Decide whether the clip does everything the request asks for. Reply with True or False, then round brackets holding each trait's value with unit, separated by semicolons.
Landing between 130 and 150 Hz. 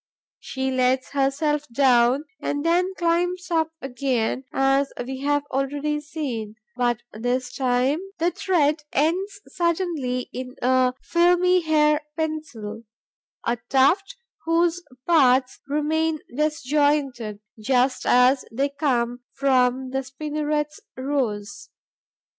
False (275 Hz)